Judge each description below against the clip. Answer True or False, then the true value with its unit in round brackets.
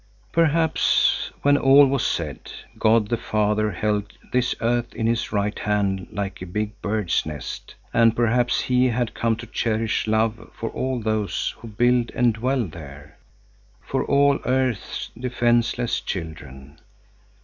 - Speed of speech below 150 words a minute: True (140 wpm)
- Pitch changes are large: False (3.1 semitones)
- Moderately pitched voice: False (115 Hz)